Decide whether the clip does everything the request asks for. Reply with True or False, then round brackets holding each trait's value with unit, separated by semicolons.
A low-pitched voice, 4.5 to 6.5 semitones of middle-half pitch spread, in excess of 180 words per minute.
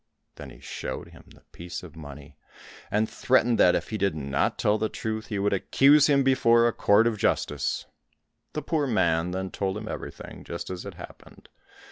True (105 Hz; 5.1 semitones; 190 wpm)